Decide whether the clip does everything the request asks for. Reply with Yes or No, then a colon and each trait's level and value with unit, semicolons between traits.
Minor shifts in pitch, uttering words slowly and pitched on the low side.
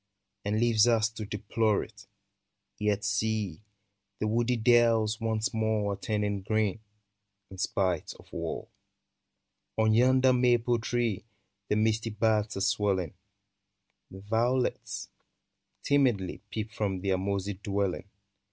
Yes: narrow, 2.1 semitones; slow, 120 wpm; low, 110 Hz